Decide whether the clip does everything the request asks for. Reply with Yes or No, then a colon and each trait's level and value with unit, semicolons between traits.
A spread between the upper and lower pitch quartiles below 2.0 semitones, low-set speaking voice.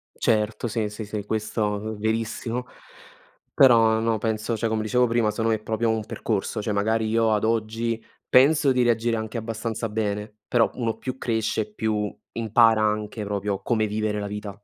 Yes: narrow, 1.3 semitones; low, 110 Hz